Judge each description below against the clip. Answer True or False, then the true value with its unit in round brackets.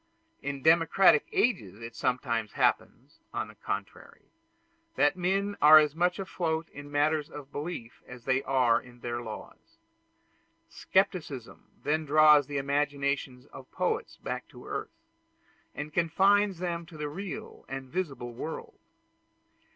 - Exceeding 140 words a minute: False (135 wpm)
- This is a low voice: False (150 Hz)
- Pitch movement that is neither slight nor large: True (4.7 semitones)